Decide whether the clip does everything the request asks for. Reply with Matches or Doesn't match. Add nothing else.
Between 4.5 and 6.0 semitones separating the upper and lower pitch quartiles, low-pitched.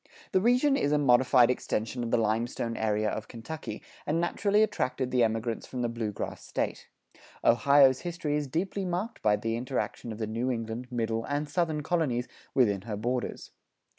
Matches